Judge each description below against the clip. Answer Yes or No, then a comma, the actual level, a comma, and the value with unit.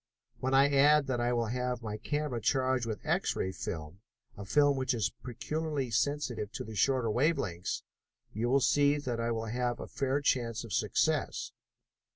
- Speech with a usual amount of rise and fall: Yes, average, 3.7 semitones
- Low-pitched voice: Yes, low, 125 Hz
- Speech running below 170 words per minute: No, average, 185 wpm